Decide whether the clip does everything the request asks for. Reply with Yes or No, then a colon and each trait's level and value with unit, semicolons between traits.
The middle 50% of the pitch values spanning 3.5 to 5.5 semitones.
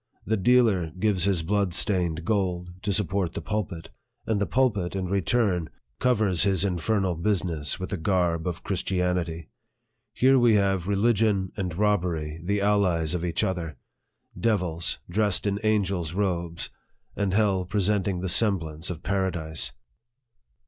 No: average, 2.9 semitones